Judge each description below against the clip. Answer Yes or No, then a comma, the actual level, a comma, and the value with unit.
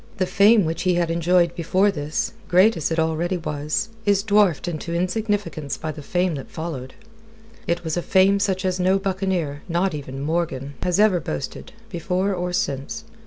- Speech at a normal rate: Yes, average, 175 wpm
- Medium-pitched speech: Yes, medium, 175 Hz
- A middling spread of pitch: Yes, average, 3.3 semitones